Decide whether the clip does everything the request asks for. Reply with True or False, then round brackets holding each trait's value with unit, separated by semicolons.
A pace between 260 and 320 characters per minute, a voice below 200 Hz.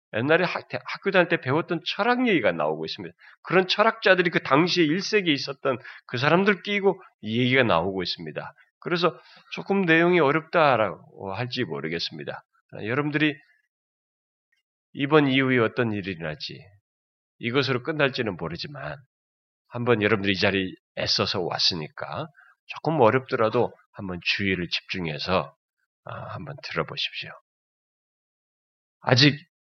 True (305 characters per minute; 135 Hz)